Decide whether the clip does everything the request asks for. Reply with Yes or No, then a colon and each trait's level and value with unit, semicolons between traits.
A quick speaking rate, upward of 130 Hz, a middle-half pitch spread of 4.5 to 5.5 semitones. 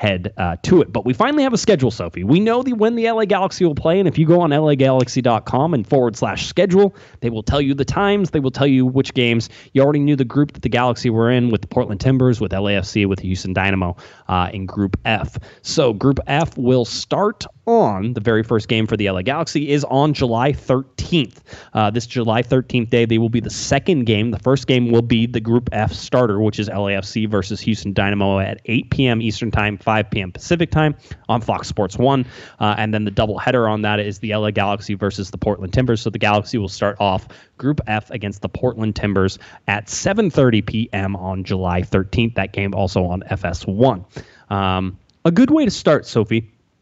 No: fast, 215 wpm; low, 115 Hz; average, 4.9 semitones